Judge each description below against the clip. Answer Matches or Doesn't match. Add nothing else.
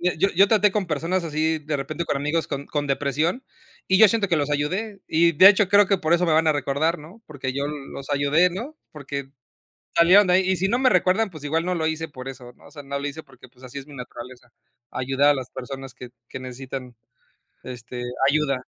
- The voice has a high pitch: Doesn't match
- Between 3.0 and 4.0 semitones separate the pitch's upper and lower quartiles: Doesn't match